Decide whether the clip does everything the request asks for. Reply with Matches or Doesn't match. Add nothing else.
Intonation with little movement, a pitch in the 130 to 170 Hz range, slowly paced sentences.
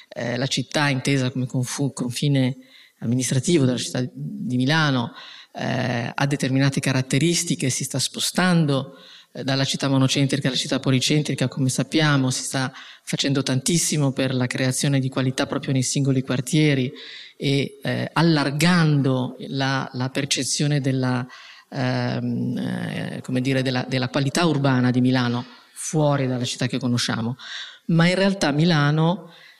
Doesn't match